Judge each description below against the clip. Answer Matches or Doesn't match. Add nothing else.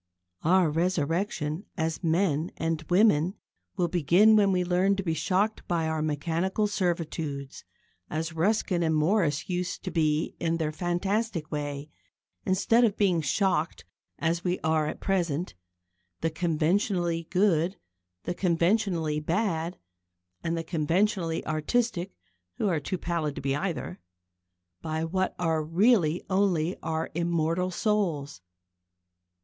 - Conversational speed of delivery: Doesn't match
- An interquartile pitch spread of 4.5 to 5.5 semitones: Doesn't match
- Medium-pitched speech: Matches